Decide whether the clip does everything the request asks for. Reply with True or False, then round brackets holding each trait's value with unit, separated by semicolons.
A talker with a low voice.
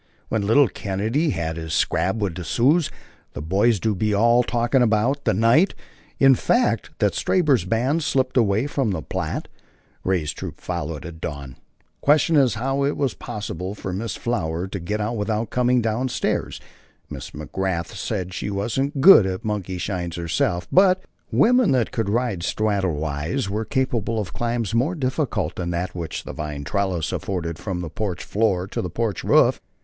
True (105 Hz)